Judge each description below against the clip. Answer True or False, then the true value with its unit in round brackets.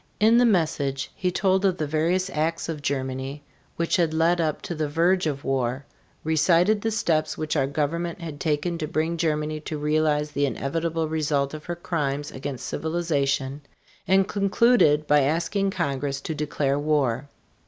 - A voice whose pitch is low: False (155 Hz)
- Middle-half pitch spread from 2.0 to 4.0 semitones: True (2.9 semitones)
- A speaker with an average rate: True (165 wpm)